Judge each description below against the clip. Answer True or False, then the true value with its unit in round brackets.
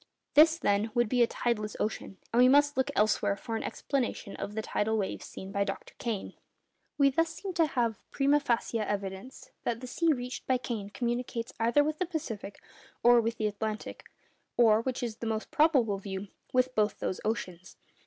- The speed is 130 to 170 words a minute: False (185 wpm)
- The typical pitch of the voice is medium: False (235 Hz)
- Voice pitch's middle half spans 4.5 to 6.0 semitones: False (3.7 semitones)